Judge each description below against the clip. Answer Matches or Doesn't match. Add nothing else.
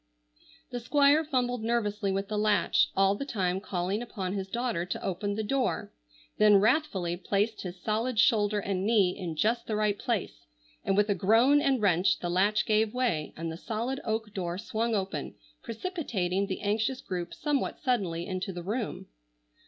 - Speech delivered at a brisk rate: Doesn't match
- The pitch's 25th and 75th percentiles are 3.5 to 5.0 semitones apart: Matches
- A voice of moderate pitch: Doesn't match